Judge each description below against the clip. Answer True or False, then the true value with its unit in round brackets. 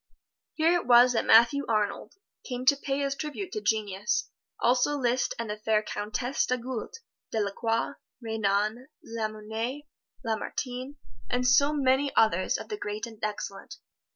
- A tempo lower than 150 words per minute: True (140 wpm)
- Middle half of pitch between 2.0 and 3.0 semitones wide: False (3.9 semitones)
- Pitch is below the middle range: False (240 Hz)